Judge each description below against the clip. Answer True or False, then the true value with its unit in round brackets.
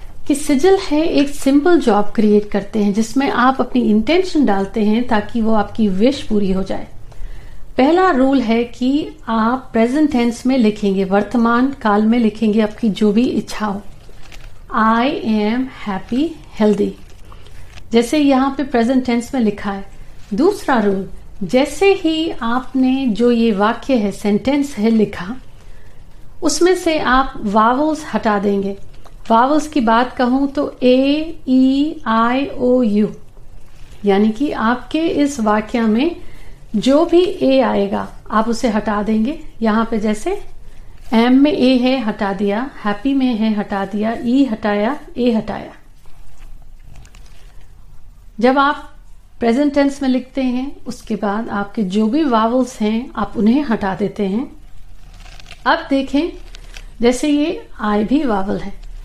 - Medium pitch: False (235 Hz)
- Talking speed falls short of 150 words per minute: True (135 wpm)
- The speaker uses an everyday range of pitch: True (4.6 semitones)